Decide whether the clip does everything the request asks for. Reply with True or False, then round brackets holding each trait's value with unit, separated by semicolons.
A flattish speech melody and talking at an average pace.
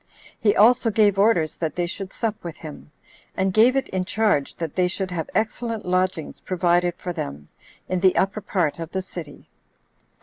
False (3.4 semitones; 180 wpm)